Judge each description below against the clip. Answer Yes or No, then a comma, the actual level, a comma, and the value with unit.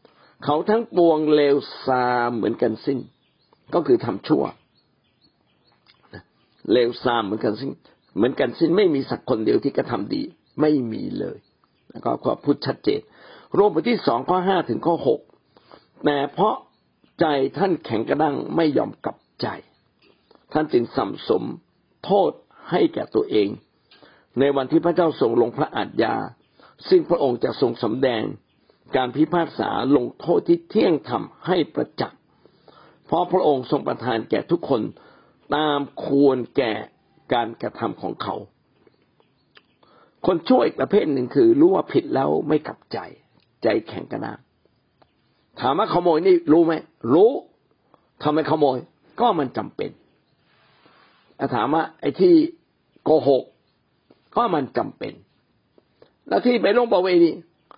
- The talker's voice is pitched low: No, medium, 155 Hz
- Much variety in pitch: Yes, wide, 6.2 semitones